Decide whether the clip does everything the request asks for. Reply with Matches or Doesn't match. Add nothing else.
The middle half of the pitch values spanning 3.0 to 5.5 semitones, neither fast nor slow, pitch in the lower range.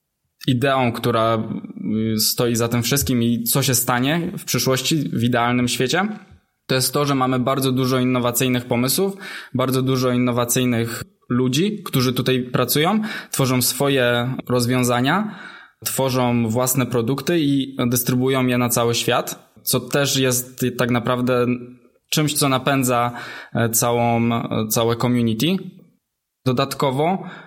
Doesn't match